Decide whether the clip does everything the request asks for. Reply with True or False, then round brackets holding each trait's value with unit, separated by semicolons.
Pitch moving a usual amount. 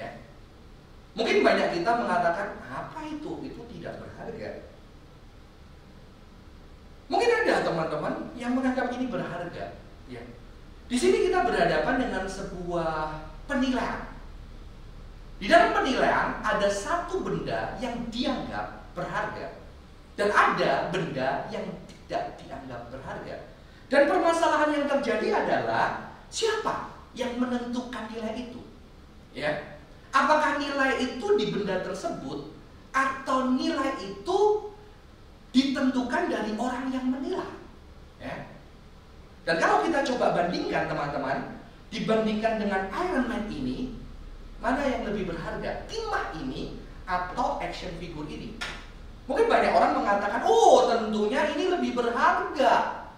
False (5.8 semitones)